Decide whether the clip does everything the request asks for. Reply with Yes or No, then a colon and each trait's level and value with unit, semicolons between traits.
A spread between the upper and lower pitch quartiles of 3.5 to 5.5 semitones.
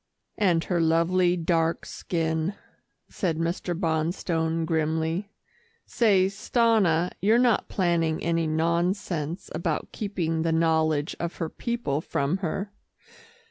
No: narrow, 2.6 semitones